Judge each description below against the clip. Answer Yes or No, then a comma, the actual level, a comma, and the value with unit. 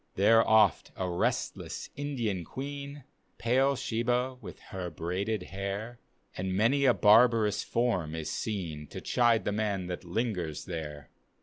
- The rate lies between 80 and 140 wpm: Yes, slow, 135 wpm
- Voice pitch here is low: Yes, low, 105 Hz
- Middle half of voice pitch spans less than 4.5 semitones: No, average, 5.1 semitones